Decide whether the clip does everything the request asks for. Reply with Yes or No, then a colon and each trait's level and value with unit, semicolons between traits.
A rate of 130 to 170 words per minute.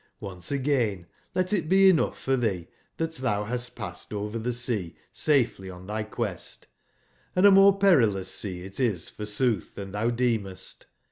Yes: average, 165 wpm